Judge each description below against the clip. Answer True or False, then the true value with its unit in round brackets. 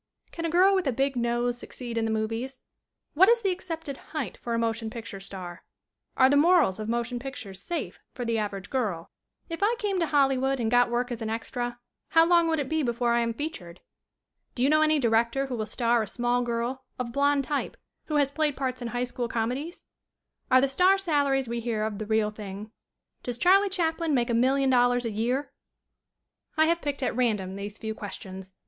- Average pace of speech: False (210 wpm)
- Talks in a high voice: True (245 Hz)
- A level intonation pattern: False (4.2 semitones)